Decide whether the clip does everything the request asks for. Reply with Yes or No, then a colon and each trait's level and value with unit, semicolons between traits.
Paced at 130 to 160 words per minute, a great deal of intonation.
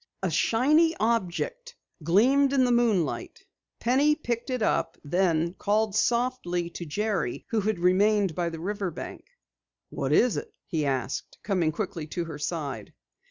Yes: average, 150 wpm; wide, 5.9 semitones